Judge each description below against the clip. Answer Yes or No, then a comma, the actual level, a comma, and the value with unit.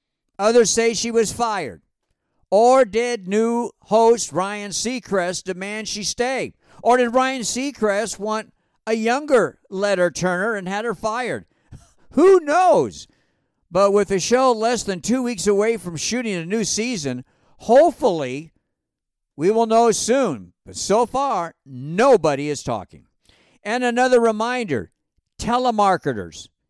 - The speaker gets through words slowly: Yes, slow, 130 wpm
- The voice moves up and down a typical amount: Yes, average, 4.8 semitones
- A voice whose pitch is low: No, high, 220 Hz